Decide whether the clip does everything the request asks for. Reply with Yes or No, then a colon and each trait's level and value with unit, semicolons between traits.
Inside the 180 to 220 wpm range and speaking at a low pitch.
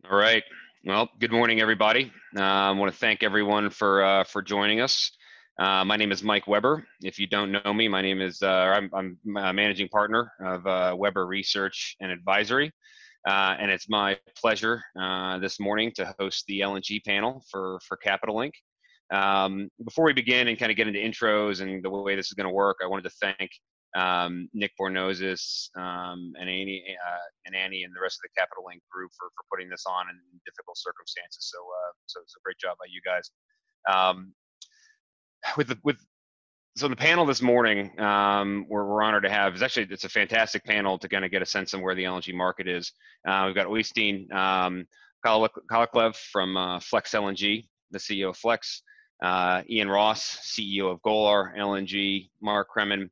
Yes: average, 195 wpm; low, 100 Hz